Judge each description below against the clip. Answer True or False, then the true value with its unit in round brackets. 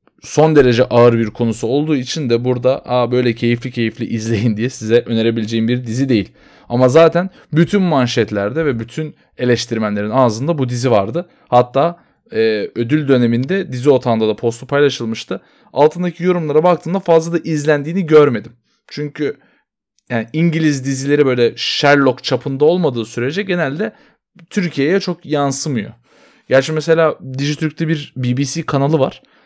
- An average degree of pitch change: True (4.8 semitones)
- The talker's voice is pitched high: False (135 Hz)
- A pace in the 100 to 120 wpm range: False (135 wpm)